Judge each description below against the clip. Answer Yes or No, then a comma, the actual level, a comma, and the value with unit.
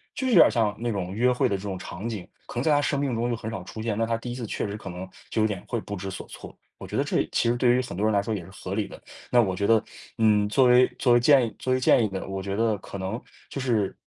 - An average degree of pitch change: Yes, average, 3.6 semitones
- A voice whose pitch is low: Yes, low, 110 Hz